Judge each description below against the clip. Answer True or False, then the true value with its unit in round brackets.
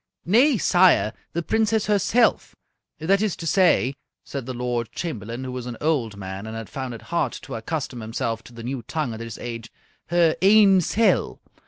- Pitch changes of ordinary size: False (8.0 semitones)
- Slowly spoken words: False (185 wpm)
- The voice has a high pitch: False (135 Hz)